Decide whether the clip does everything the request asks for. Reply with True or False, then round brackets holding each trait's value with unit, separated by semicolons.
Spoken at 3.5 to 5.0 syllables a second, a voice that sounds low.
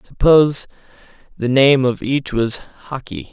True (4.5 syllables/s; 130 Hz)